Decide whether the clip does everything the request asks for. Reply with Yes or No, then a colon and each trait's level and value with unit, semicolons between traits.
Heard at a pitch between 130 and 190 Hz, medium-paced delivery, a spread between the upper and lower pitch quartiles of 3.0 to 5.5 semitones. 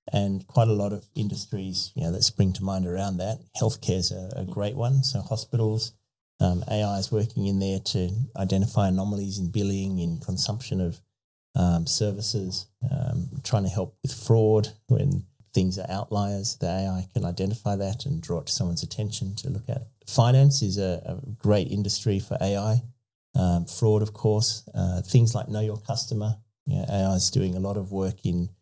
No: low, 105 Hz; average, 190 wpm; average, 3.3 semitones